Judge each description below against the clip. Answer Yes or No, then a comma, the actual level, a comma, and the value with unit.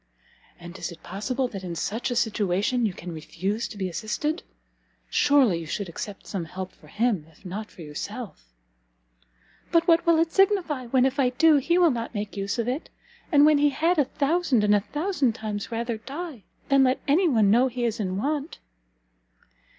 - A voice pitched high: Yes, high, 235 Hz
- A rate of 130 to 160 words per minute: No, average, 195 wpm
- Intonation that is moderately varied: No, wide, 6.5 semitones